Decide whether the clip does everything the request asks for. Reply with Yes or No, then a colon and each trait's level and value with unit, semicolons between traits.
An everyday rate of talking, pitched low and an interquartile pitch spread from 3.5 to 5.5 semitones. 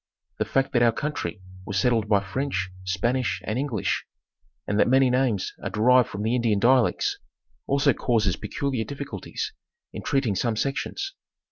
Yes: average, 155 wpm; low, 120 Hz; average, 4.2 semitones